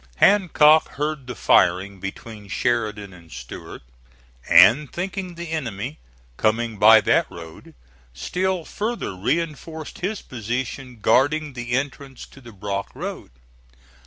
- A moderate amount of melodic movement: No, wide, 7.2 semitones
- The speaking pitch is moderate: No, low, 125 Hz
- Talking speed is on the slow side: Yes, slow, 120 wpm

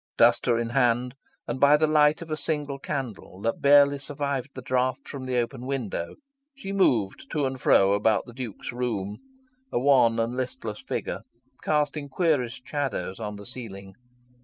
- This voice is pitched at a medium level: No, low, 130 Hz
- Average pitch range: Yes, average, 3.6 semitones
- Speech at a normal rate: Yes, average, 165 wpm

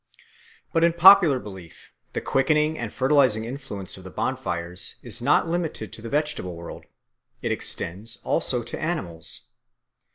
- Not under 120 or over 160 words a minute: Yes, average, 140 wpm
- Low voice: Yes, low, 120 Hz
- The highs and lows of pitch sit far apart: Yes, wide, 8.4 semitones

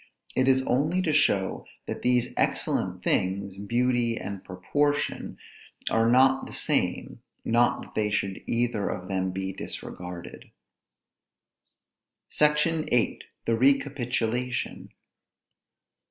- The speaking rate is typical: No, slow, 110 wpm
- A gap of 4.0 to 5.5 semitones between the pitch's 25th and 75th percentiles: Yes, average, 5.1 semitones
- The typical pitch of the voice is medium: No, low, 120 Hz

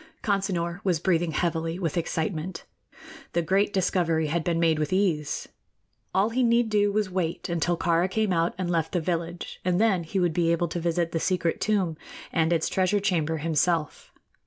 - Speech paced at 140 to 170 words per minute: No, average, 185 wpm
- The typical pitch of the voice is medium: Yes, medium, 175 Hz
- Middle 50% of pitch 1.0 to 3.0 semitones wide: Yes, narrow, 2.5 semitones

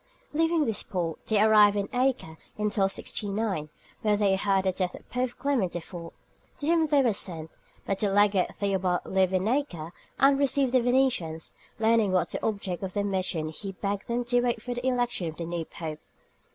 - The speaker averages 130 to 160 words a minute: No, average, 200 wpm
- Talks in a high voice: Yes, high, 205 Hz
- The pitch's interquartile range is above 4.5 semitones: Yes, average, 5.0 semitones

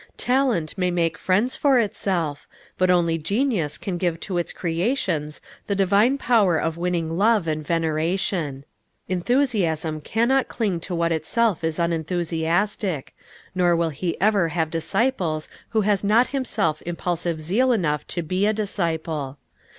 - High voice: No, medium, 175 Hz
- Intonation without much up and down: No, average, 4.3 semitones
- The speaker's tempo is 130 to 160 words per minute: Yes, average, 145 wpm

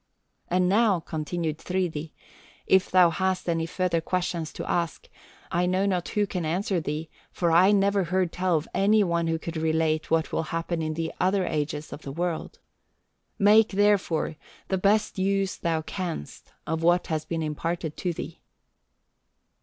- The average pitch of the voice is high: No, medium, 175 Hz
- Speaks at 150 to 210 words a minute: Yes, average, 165 wpm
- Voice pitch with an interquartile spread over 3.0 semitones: No, average, 2.7 semitones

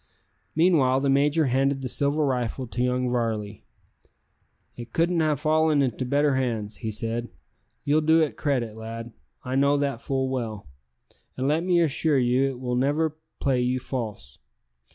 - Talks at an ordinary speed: Yes, average, 160 wpm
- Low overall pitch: Yes, low, 130 Hz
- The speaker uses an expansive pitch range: No, average, 3.3 semitones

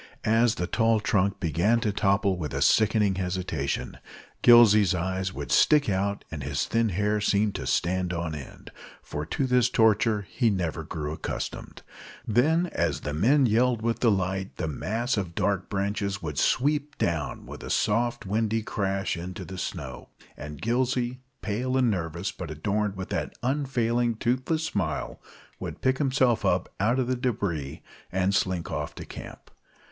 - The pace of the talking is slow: No, average, 160 wpm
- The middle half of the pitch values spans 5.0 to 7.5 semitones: No, average, 4.5 semitones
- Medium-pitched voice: No, low, 105 Hz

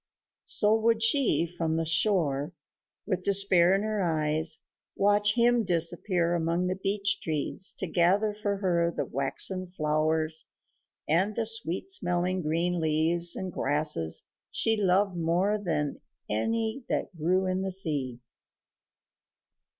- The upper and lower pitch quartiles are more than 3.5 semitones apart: Yes, average, 4.0 semitones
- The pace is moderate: No, slow, 130 wpm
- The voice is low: No, medium, 180 Hz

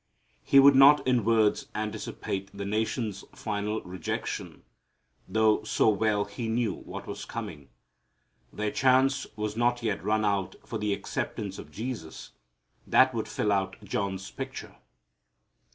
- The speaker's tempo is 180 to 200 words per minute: No, slow, 135 wpm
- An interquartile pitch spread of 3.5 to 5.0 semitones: No, average, 2.8 semitones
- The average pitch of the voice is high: No, low, 105 Hz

